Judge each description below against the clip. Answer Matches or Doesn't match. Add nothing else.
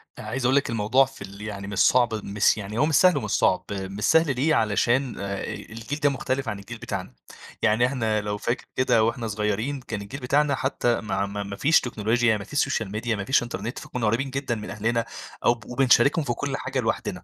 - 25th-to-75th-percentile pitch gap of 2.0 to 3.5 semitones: Doesn't match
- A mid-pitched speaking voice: Doesn't match